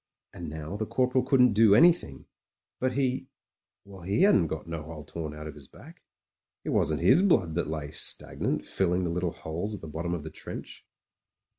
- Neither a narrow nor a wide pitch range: No, wide, 7.2 semitones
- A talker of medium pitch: No, very low, 90 Hz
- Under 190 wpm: No, average, 195 wpm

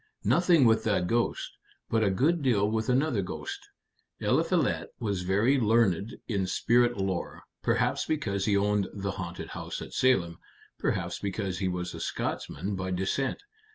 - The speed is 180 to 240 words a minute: No, average, 155 wpm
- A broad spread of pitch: No, average, 4.1 semitones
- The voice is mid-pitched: No, low, 105 Hz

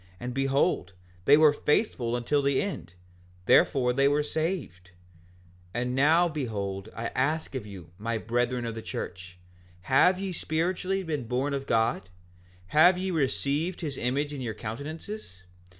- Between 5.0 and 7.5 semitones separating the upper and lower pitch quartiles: Yes, average, 5.3 semitones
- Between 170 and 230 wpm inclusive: No, average, 150 wpm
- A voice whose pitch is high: No, low, 135 Hz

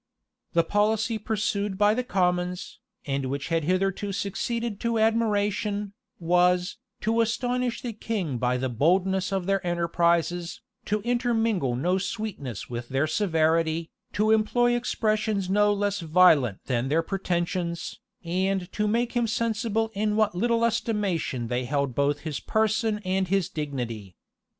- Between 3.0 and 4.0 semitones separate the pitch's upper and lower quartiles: No, average, 4.7 semitones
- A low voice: No, high, 190 Hz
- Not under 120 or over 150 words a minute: Yes, average, 140 wpm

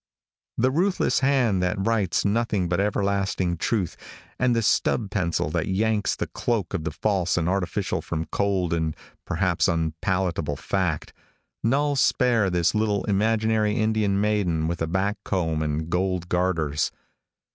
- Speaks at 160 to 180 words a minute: No, average, 145 wpm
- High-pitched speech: No, very low, 95 Hz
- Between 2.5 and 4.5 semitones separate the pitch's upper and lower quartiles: Yes, average, 3.9 semitones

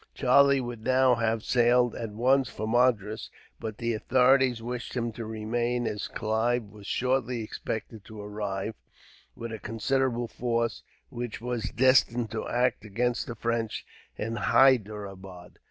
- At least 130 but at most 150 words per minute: Yes, average, 140 wpm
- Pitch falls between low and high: No, low, 115 Hz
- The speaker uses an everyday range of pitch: No, narrow, 2.2 semitones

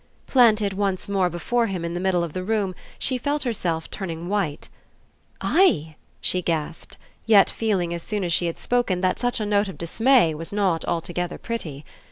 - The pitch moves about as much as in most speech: Yes, average, 4.3 semitones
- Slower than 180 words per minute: No, average, 185 wpm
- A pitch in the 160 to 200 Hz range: Yes, high, 190 Hz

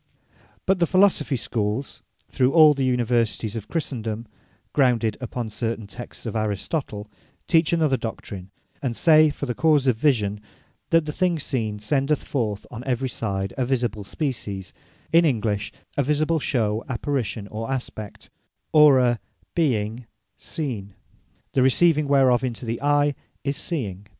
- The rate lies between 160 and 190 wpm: No, average, 140 wpm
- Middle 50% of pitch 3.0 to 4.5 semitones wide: No, average, 5.0 semitones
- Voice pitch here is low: Yes, low, 125 Hz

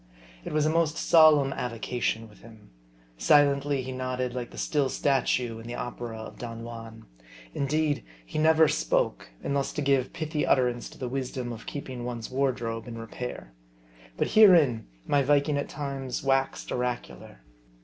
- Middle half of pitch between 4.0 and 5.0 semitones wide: No, average, 3.2 semitones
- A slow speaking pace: No, average, 160 wpm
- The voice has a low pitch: Yes, low, 130 Hz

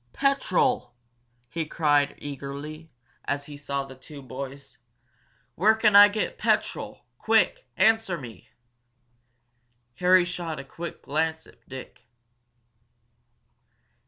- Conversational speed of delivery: No, slow, 105 wpm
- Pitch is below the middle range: No, medium, 155 Hz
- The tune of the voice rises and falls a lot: No, average, 5.0 semitones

